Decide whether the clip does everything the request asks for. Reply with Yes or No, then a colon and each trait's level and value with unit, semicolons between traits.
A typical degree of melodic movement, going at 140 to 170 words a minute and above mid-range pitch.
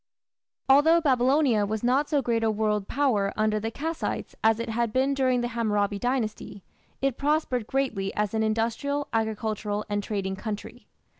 Yes: average, 4.1 semitones; average, 160 wpm; high, 225 Hz